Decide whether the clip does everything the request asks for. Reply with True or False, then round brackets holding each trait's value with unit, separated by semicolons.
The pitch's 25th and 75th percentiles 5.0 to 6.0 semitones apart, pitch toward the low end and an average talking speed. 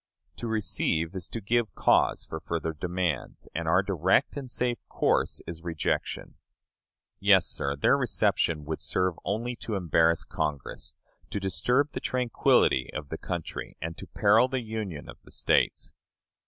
True (5.6 semitones; 90 Hz; 155 wpm)